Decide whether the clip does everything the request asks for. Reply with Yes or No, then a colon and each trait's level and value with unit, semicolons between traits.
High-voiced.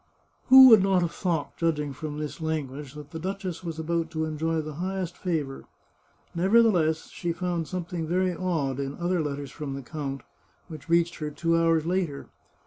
No: medium, 165 Hz